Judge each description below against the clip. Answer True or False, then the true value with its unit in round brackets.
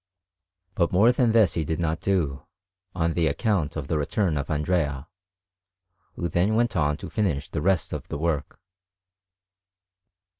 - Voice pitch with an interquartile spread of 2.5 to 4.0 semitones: False (4.4 semitones)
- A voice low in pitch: True (80 Hz)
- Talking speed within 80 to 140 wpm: False (150 wpm)